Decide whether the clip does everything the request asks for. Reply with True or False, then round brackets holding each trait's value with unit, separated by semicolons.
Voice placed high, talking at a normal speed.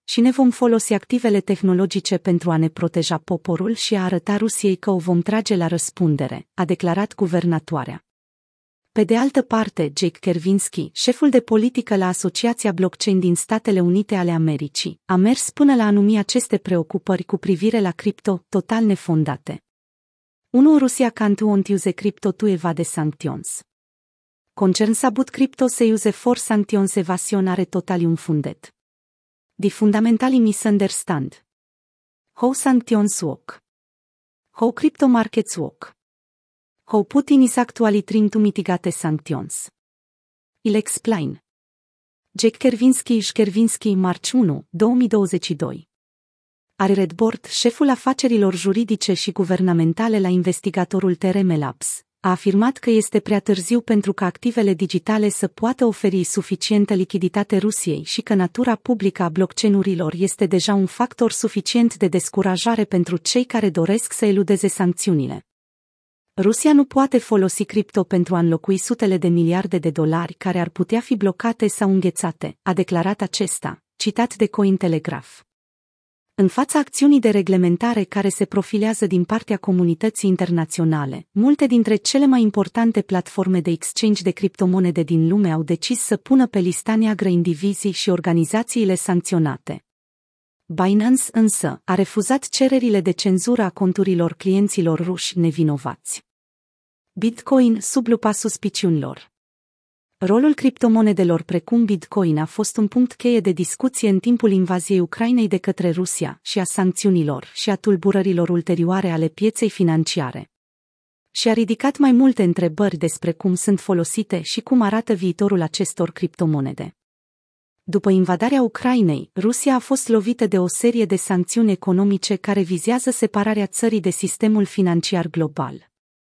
True (200 Hz; 140 wpm)